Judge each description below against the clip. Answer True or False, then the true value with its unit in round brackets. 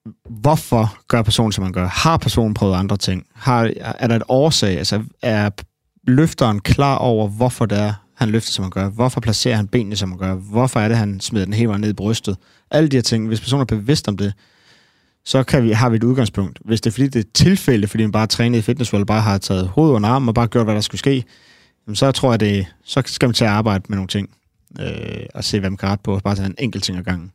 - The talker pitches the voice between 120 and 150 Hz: False (110 Hz)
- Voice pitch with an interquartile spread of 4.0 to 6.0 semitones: False (3.5 semitones)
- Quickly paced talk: True (265 wpm)